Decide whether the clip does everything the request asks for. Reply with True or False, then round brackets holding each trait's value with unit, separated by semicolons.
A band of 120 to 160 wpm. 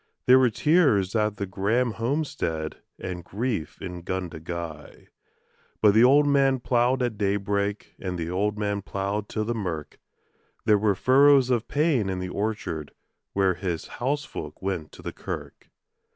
True (150 wpm)